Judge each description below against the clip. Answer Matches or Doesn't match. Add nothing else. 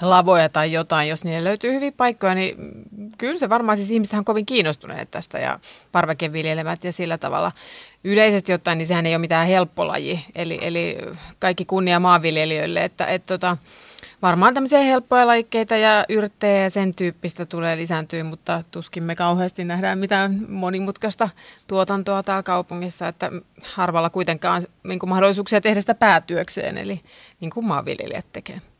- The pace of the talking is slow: Doesn't match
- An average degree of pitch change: Matches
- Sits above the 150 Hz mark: Matches